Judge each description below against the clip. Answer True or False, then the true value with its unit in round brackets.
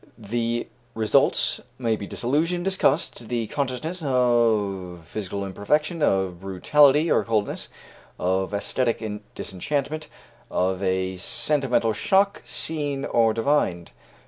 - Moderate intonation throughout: False (6.8 semitones)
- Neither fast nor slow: False (105 wpm)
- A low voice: True (115 Hz)